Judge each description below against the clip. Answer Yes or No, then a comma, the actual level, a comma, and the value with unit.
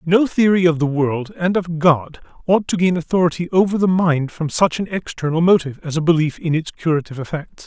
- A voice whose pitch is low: No, medium, 165 Hz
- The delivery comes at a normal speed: No, fast, 210 wpm